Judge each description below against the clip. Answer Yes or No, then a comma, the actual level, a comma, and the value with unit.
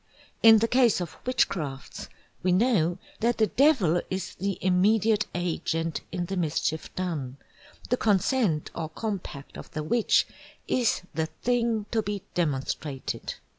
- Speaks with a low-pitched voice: No, medium, 185 Hz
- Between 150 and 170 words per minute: No, slow, 135 wpm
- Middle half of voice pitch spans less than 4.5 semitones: No, wide, 5.5 semitones